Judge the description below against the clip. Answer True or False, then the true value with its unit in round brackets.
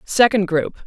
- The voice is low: False (195 Hz)